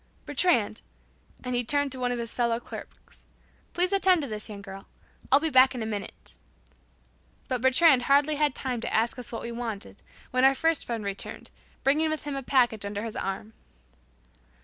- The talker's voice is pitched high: Yes, very high, 250 Hz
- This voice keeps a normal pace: Yes, average, 190 wpm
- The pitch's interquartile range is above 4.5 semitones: No, average, 4.2 semitones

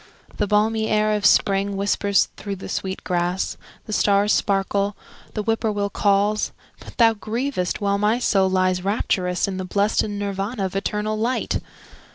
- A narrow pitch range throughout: Yes, narrow, 1.7 semitones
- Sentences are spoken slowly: No, average, 155 wpm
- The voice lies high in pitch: Yes, high, 200 Hz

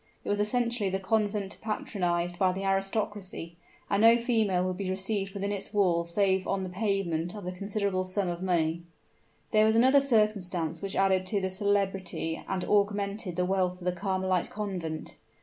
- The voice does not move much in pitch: Yes, narrow, 2.2 semitones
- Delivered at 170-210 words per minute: Yes, average, 175 wpm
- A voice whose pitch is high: Yes, high, 195 Hz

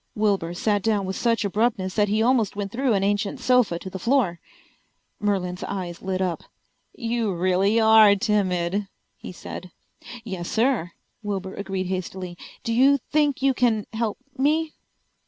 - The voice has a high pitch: Yes, high, 205 Hz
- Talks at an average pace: Yes, average, 155 wpm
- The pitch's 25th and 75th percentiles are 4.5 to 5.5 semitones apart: No, average, 3.6 semitones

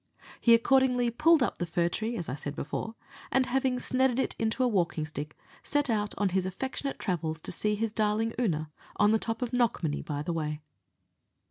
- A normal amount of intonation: No, wide, 6.7 semitones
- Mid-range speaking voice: No, high, 220 Hz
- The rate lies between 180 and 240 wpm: Yes, average, 200 wpm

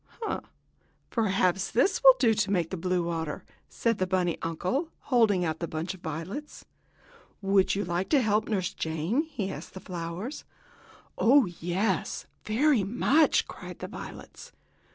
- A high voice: Yes, high, 195 Hz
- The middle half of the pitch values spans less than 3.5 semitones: No, average, 5.2 semitones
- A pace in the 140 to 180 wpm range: Yes, average, 150 wpm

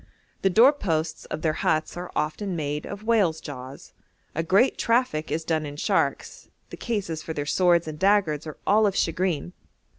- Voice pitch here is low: No, medium, 165 Hz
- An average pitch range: Yes, average, 4.4 semitones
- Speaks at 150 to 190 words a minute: Yes, average, 180 wpm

